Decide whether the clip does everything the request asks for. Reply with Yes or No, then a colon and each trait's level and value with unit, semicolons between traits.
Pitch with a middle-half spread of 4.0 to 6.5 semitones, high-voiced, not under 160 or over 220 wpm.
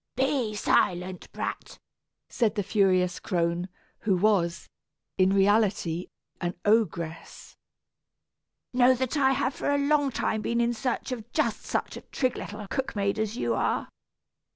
No: average, 5.1 semitones; high, 215 Hz; average, 145 wpm